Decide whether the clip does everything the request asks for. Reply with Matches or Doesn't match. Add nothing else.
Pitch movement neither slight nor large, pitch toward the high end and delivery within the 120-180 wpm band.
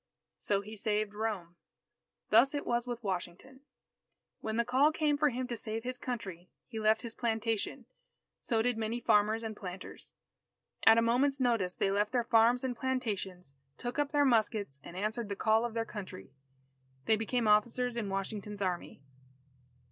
Matches